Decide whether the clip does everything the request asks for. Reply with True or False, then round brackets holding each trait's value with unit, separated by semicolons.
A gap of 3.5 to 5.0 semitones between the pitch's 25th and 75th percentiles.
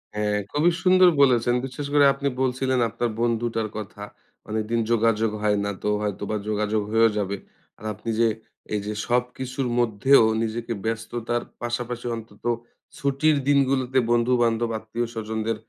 False (2.6 semitones)